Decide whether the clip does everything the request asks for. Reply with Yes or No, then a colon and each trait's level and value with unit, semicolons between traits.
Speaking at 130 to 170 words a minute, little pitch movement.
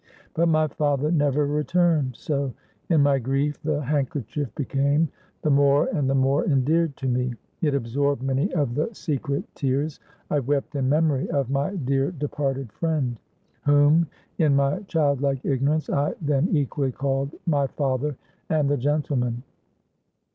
Yes: average, 150 wpm; narrow, 1.8 semitones